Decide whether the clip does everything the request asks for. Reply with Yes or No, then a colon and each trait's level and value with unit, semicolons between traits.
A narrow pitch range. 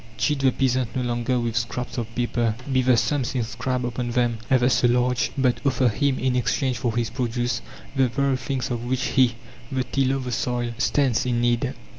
Yes: narrow, 1.5 semitones